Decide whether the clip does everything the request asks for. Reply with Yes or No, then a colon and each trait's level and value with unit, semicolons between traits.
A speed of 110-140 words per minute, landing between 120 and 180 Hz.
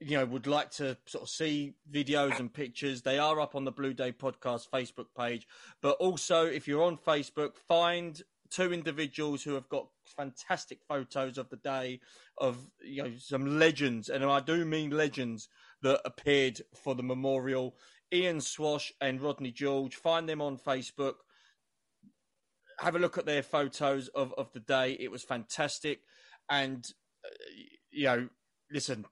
No: average, 165 wpm; medium, 140 Hz